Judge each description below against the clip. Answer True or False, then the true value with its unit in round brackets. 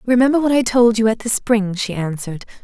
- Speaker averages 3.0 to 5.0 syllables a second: False (6.0 syllables/s)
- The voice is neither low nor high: False (225 Hz)